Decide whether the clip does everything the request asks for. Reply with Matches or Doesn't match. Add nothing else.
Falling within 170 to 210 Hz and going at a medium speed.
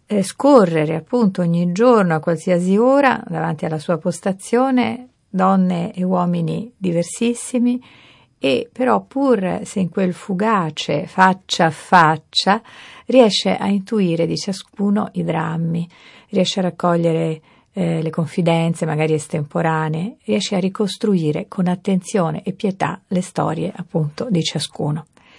Matches